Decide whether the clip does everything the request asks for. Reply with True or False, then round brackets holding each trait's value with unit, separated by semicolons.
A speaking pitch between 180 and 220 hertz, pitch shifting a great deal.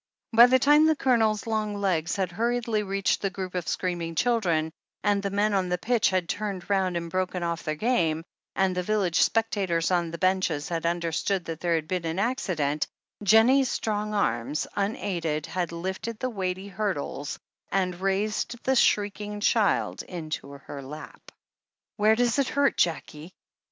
False (190 Hz; 4.1 semitones)